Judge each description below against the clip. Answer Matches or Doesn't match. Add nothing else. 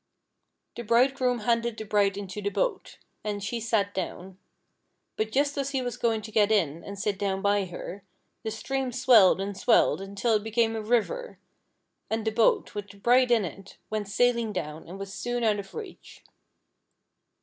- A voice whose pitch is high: Matches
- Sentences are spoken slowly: Doesn't match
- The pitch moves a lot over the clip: Doesn't match